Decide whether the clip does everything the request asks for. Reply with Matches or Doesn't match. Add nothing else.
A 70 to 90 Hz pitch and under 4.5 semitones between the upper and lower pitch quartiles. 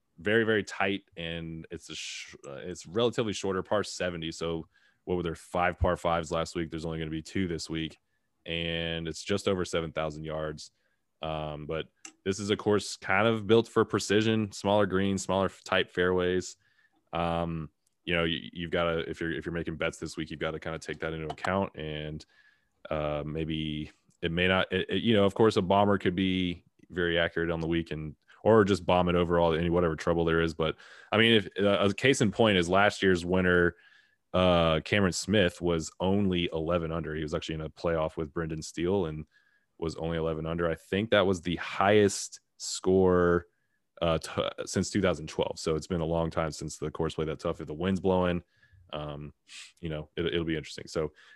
Matches